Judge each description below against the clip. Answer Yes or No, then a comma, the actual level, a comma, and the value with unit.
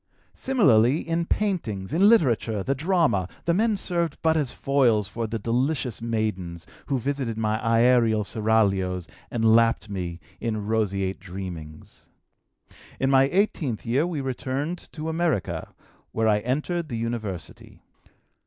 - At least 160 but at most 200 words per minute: No, slow, 135 wpm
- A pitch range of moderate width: No, wide, 6.4 semitones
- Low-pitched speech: Yes, low, 115 Hz